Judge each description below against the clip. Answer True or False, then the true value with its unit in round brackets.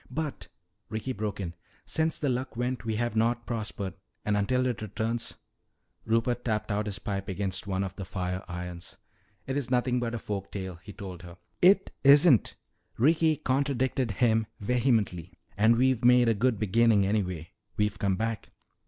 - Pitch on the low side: True (110 Hz)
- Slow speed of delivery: False (170 wpm)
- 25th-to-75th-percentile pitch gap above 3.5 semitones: True (3.9 semitones)